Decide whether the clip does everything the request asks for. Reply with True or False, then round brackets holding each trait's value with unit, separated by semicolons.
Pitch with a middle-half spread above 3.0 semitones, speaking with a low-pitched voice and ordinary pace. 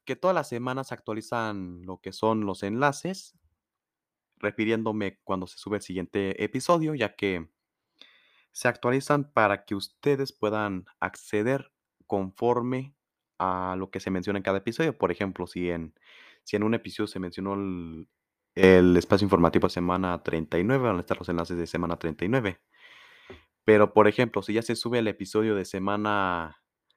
True (4.0 semitones; 100 Hz; 160 wpm)